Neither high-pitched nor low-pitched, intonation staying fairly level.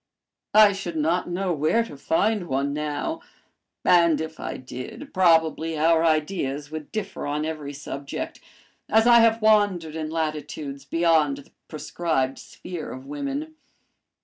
No: medium, 160 Hz; average, 4.7 semitones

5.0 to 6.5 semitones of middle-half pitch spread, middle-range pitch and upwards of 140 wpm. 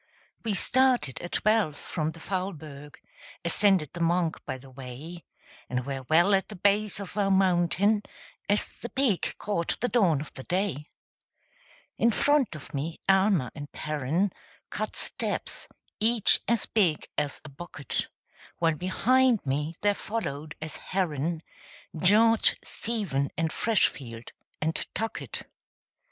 No: wide, 5.6 semitones; medium, 175 Hz; slow, 135 wpm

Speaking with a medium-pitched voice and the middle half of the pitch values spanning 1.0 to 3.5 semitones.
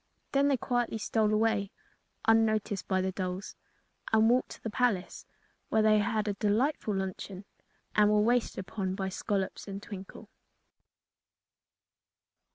No: high, 210 Hz; narrow, 2.5 semitones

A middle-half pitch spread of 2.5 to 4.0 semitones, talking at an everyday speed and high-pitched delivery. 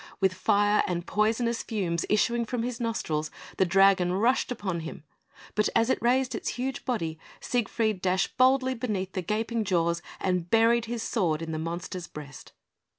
No: average, 5.0 semitones; average, 165 wpm; high, 205 Hz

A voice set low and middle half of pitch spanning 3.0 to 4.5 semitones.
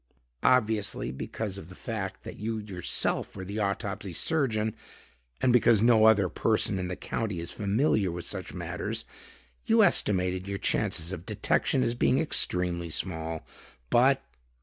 Yes: low, 100 Hz; average, 3.5 semitones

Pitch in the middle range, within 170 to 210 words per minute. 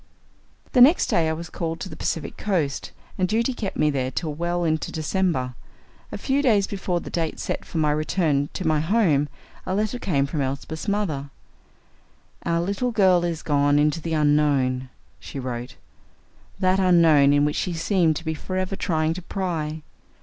Yes: medium, 165 Hz; average, 180 wpm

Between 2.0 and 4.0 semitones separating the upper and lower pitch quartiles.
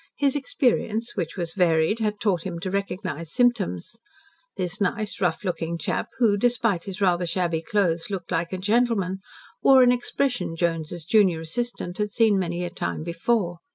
No: average, 4.7 semitones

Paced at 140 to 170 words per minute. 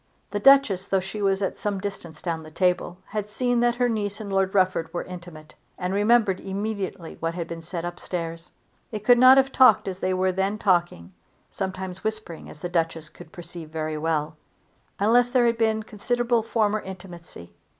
No: average, 190 wpm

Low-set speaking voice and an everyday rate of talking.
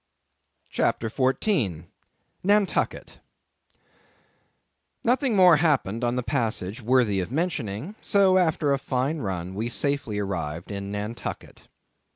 No: low, 125 Hz; slow, 110 wpm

